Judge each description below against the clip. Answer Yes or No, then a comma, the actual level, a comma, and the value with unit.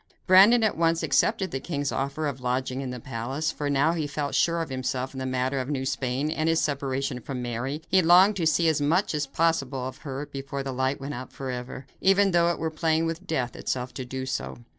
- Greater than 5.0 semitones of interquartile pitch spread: No, average, 3.8 semitones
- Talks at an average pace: No, fast, 235 wpm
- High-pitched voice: No, medium, 140 Hz